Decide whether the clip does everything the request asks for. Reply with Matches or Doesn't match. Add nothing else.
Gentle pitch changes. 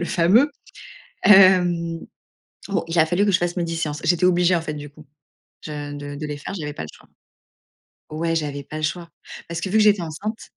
Doesn't match